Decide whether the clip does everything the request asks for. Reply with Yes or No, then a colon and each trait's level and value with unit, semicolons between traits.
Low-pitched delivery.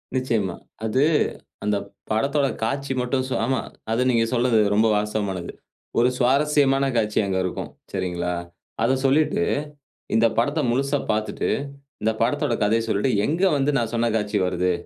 Yes: low, 115 Hz